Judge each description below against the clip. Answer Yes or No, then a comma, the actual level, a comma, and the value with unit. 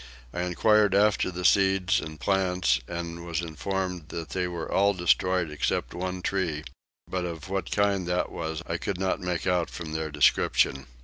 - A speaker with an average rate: Yes, average, 175 wpm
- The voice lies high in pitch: No, very low, 90 Hz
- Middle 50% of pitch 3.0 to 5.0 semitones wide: No, narrow, 2.4 semitones